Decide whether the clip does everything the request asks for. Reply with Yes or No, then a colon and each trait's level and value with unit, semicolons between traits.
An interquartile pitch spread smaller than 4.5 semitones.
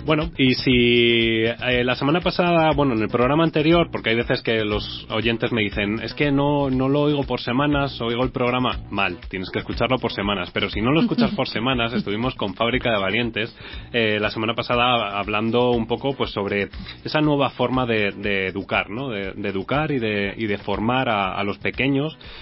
Yes: average, 4.1 semitones